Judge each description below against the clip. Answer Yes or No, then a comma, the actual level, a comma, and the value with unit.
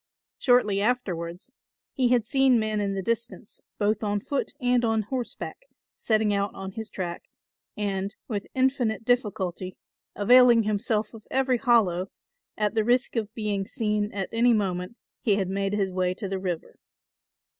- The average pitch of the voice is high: Yes, high, 215 Hz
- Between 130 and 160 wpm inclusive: Yes, average, 155 wpm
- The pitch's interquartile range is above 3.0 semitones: Yes, average, 3.5 semitones